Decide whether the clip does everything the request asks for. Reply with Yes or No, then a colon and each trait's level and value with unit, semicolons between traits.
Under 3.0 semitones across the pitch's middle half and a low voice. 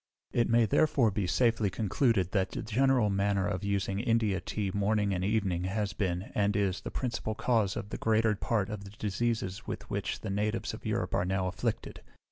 Yes: narrow, 2.5 semitones; low, 105 Hz